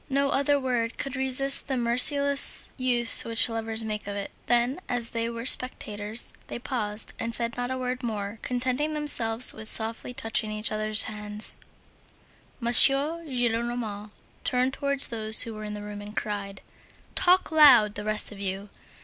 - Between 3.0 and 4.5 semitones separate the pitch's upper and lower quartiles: Yes, average, 3.3 semitones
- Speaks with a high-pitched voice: Yes, high, 235 Hz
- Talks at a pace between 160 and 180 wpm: Yes, average, 165 wpm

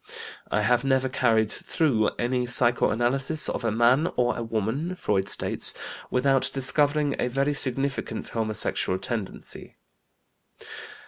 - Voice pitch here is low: Yes, low, 125 Hz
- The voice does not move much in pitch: No, average, 3.3 semitones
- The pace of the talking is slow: Yes, slow, 120 wpm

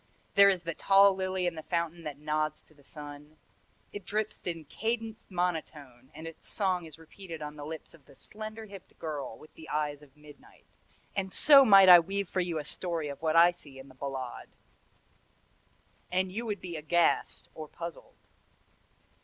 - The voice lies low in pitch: No, medium, 165 Hz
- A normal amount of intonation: Yes, average, 4.0 semitones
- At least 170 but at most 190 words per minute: Yes, average, 185 wpm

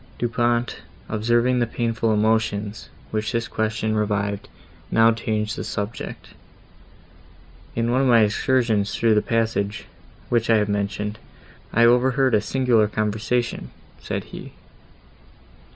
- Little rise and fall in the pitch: Yes, narrow, 1.9 semitones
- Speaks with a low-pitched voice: Yes, low, 110 Hz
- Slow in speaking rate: Yes, slow, 125 wpm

